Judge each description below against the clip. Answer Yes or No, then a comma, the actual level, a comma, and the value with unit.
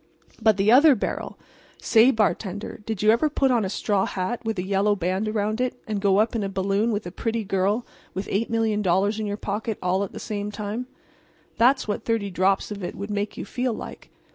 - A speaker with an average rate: No, fast, 215 wpm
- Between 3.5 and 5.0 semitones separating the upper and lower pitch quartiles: No, narrow, 2.4 semitones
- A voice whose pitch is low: No, high, 210 Hz